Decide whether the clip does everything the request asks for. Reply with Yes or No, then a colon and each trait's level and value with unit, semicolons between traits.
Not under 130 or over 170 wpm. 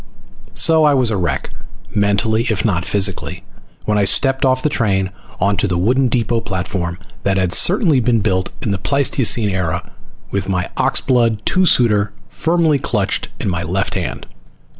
Yes: average, 160 wpm